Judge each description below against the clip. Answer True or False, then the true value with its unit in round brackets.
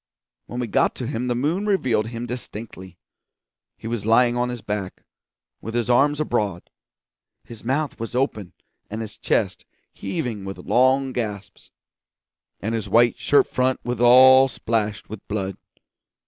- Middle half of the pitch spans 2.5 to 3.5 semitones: True (3.0 semitones)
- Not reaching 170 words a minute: True (150 wpm)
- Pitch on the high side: False (120 Hz)